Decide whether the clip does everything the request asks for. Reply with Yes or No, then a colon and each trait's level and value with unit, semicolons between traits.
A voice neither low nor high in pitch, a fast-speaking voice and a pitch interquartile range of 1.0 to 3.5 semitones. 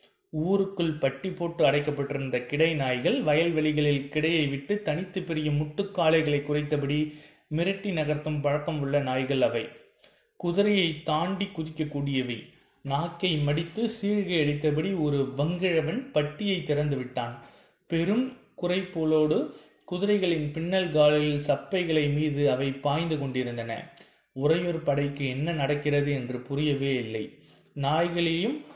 No: medium, 155 Hz; average, 100 wpm; average, 3.2 semitones